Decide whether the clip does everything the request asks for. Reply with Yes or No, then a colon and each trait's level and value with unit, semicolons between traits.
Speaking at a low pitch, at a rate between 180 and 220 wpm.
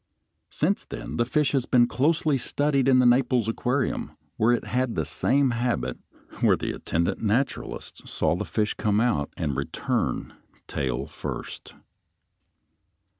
No: low, 120 Hz; average, 145 wpm